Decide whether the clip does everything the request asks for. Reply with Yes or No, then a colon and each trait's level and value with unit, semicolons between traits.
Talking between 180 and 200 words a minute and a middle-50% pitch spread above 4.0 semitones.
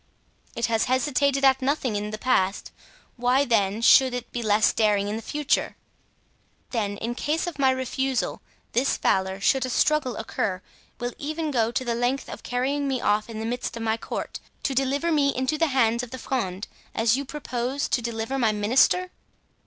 No: average, 185 wpm; average, 3.4 semitones